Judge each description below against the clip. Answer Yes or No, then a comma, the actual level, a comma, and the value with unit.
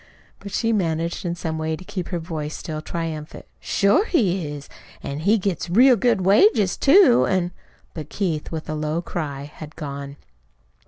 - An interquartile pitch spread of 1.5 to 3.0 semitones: No, average, 4.4 semitones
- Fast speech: No, average, 175 wpm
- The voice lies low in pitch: No, medium, 170 Hz